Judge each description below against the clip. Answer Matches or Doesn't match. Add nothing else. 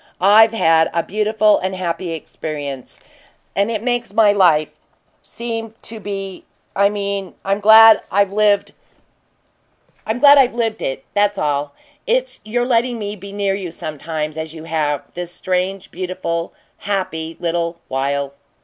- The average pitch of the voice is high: Matches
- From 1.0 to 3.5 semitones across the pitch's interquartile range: Doesn't match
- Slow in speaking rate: Matches